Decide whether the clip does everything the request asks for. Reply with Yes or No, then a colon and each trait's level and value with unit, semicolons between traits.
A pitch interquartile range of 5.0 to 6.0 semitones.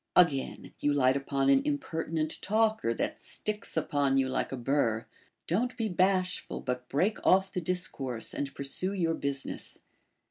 Yes: average, 5.3 semitones